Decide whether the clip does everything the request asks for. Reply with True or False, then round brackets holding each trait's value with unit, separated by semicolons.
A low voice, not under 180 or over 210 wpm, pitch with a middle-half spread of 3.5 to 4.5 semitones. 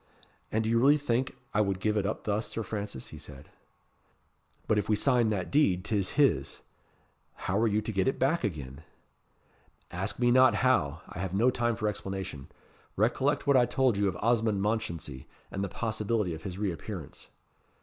True (105 Hz; 190 wpm; 3.9 semitones)